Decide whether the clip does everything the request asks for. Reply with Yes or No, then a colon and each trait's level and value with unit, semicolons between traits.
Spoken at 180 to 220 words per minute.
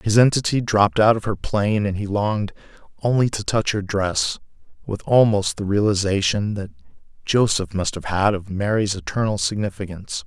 No: average, 165 wpm